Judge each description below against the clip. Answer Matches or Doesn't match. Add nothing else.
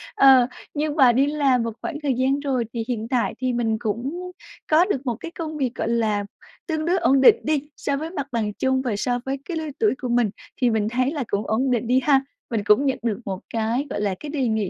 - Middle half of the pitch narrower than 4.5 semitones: Matches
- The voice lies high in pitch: Matches